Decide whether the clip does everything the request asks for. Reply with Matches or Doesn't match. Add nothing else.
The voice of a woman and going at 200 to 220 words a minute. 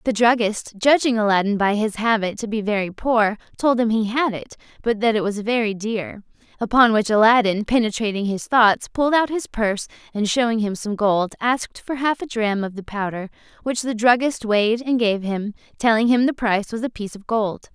Matches